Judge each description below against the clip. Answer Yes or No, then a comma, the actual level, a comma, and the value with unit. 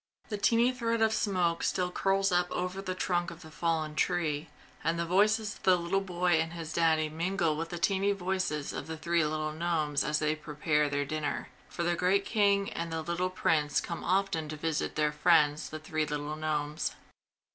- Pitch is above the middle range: No, medium, 170 Hz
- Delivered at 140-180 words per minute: No, average, 200 wpm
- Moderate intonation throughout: Yes, average, 3.2 semitones